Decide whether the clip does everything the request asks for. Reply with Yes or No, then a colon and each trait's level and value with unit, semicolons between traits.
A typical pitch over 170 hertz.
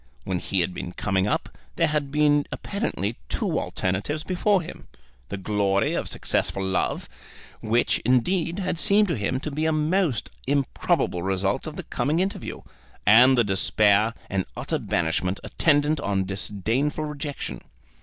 No: low, 130 Hz